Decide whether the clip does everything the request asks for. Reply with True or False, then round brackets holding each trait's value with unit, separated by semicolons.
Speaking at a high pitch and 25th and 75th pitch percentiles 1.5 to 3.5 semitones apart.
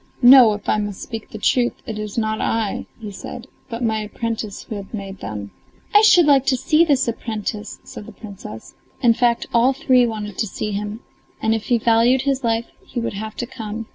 True (225 Hz; 2.6 semitones)